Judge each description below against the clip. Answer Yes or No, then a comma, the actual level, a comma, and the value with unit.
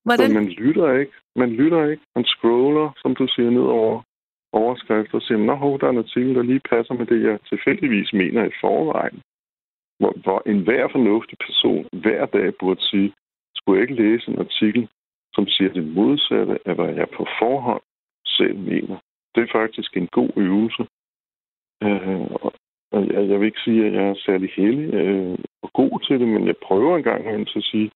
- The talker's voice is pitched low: Yes, low, 110 Hz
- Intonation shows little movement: No, average, 3.6 semitones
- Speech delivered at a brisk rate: No, average, 185 wpm